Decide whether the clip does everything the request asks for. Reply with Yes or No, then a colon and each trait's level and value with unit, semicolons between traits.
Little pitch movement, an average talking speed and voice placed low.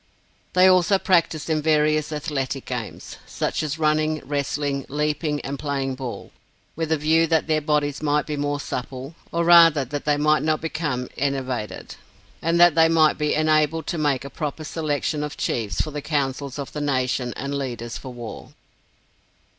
No: narrow, 2.2 semitones; average, 170 wpm; medium, 150 Hz